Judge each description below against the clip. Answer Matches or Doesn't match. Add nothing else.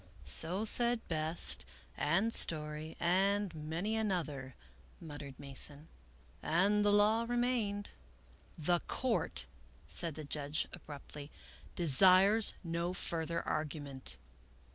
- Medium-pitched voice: Matches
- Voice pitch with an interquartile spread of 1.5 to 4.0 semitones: Doesn't match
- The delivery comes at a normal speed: Doesn't match